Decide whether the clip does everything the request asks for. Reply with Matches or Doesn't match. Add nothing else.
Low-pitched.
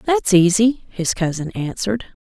Doesn't match